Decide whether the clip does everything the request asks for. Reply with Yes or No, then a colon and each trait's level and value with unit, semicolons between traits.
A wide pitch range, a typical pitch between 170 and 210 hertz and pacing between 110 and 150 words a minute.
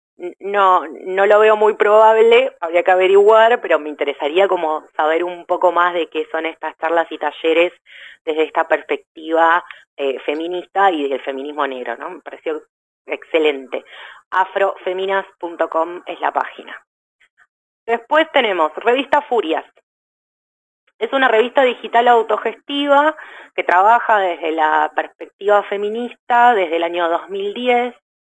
Yes: wide, 6.2 semitones; medium, 185 Hz; slow, 125 wpm